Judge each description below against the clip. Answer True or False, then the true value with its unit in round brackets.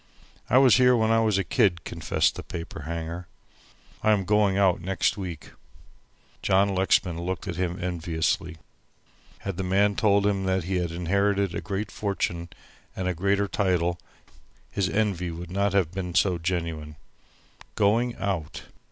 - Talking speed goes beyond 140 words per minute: True (160 wpm)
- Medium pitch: False (95 Hz)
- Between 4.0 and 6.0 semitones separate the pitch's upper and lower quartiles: False (2.7 semitones)